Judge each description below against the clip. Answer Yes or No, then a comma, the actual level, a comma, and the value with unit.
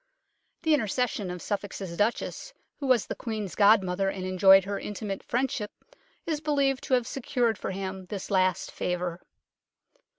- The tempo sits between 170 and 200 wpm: No, average, 145 wpm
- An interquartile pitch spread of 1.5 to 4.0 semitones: No, average, 4.7 semitones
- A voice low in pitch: No, high, 205 Hz